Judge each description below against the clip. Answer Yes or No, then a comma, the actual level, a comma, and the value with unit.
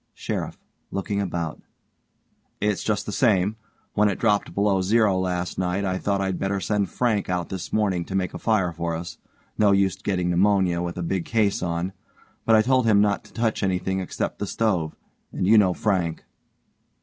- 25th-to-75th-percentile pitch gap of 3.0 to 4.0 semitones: No, narrow, 2.5 semitones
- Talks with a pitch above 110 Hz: No, very low, 95 Hz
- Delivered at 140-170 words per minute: No, average, 185 wpm